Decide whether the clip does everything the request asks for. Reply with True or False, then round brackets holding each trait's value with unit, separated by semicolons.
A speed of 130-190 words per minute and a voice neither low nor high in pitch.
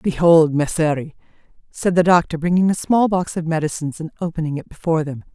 True (180 wpm; 165 Hz)